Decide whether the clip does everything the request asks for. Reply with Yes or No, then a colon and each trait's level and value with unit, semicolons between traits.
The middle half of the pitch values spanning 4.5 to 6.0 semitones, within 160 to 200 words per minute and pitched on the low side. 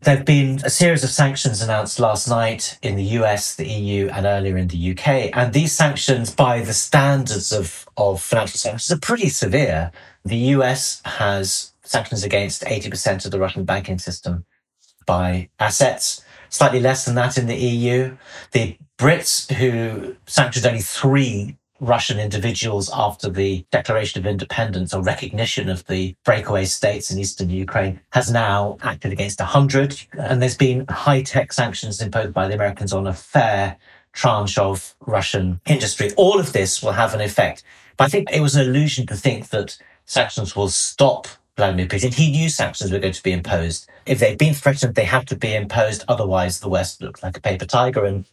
Yes: average, 5.3 semitones; average, 180 wpm; low, 110 Hz